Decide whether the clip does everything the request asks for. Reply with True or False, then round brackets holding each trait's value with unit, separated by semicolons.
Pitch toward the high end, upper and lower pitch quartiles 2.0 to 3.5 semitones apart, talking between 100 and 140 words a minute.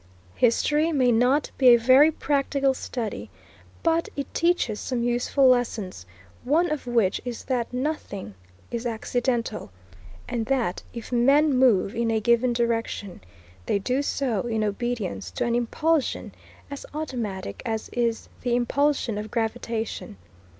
True (240 Hz; 3.2 semitones; 135 wpm)